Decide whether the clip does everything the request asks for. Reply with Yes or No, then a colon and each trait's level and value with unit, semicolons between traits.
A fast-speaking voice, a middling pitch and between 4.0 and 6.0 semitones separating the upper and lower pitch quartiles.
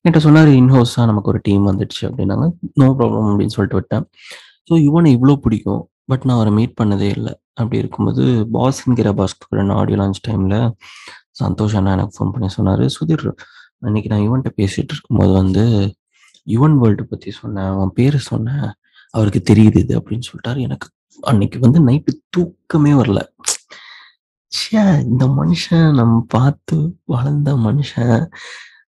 No: fast, 145 wpm; low, 115 Hz; wide, 5.4 semitones